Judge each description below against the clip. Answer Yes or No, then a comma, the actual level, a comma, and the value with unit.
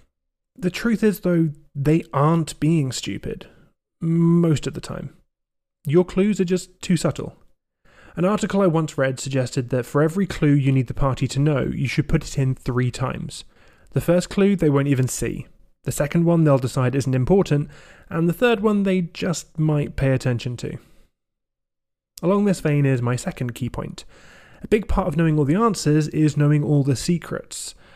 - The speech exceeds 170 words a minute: Yes, average, 185 wpm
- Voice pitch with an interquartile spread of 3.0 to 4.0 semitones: No, average, 4.6 semitones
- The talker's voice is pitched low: No, medium, 155 Hz